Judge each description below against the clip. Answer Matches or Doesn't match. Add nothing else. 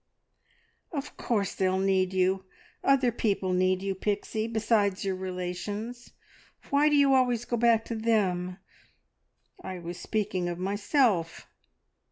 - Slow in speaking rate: Matches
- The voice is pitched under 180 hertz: Doesn't match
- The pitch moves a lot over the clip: Doesn't match